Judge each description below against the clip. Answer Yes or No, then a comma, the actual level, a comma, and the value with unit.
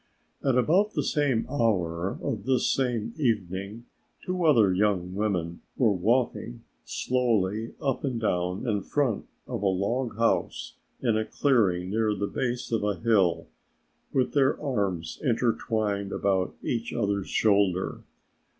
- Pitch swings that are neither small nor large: Yes, average, 4.4 semitones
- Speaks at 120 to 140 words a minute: Yes, slow, 135 wpm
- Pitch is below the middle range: Yes, low, 110 Hz